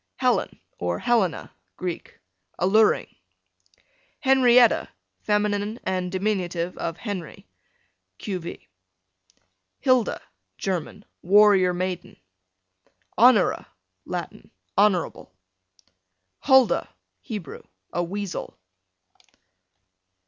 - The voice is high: Yes, high, 195 Hz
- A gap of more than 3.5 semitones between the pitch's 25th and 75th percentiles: No, average, 3.2 semitones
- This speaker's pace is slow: Yes, slow, 70 wpm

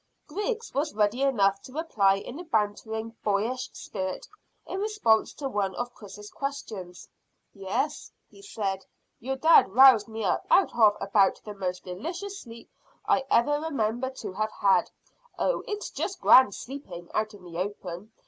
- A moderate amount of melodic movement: No, wide, 5.7 semitones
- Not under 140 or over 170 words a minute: Yes, average, 160 wpm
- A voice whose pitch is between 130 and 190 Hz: No, high, 220 Hz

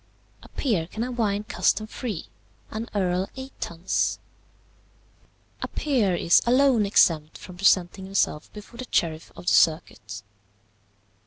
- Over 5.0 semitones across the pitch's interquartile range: Yes, wide, 5.4 semitones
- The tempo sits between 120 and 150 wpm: Yes, slow, 135 wpm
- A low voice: No, high, 195 Hz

